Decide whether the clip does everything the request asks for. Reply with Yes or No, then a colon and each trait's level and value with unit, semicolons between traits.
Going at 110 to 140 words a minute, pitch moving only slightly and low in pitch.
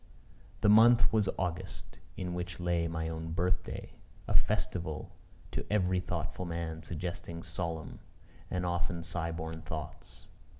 Yes: slow, 135 wpm; narrow, 1.8 semitones; very low, 85 Hz